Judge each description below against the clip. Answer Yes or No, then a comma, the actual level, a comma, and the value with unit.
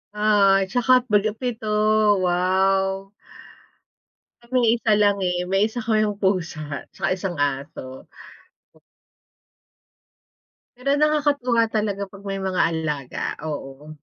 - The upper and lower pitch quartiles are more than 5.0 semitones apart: No, average, 3.5 semitones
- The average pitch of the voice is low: No, high, 195 Hz